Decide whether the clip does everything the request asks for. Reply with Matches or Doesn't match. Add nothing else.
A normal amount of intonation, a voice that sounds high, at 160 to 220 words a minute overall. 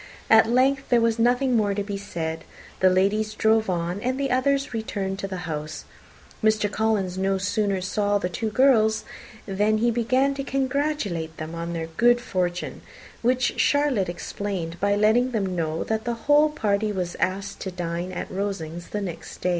Matches